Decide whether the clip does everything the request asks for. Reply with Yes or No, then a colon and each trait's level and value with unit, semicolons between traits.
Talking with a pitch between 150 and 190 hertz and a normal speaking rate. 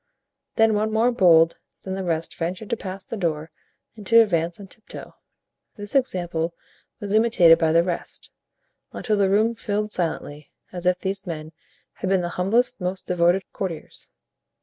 Yes: medium, 185 Hz; average, 165 wpm